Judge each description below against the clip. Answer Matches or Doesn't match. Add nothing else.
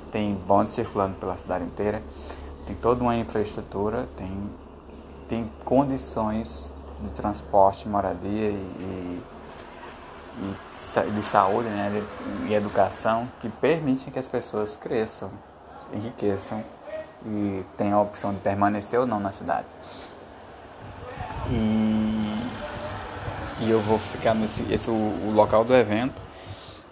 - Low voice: Matches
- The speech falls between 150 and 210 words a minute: Doesn't match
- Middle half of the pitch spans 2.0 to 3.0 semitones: Matches